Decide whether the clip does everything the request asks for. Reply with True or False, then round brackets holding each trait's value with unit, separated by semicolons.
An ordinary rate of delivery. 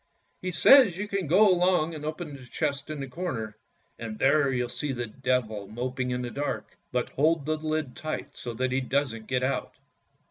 False (210 wpm)